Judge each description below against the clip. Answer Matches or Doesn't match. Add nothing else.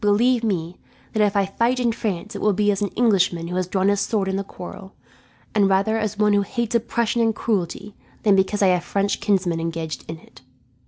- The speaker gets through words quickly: Matches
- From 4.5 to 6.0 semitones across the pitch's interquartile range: Doesn't match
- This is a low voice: Doesn't match